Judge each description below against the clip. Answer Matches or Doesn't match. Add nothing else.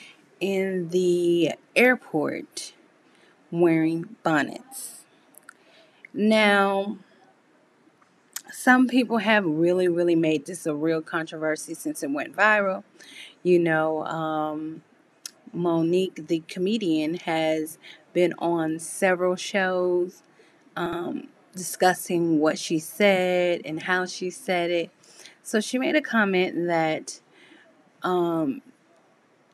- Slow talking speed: Matches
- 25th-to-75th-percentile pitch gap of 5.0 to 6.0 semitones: Doesn't match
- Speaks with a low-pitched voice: Doesn't match